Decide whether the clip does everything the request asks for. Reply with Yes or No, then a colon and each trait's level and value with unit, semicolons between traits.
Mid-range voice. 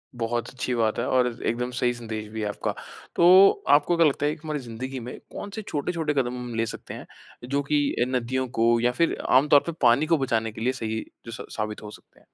No: low, 125 Hz